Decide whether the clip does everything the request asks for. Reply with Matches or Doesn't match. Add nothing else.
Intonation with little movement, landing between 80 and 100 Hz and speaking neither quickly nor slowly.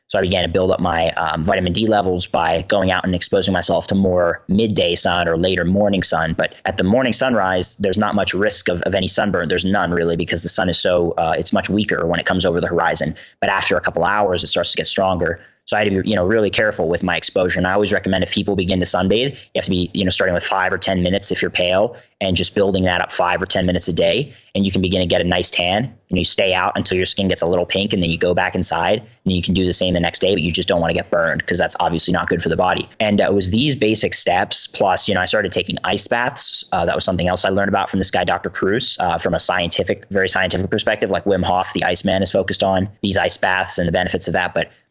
Doesn't match